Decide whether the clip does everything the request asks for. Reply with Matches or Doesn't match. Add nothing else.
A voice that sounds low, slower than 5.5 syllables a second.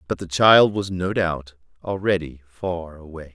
Matches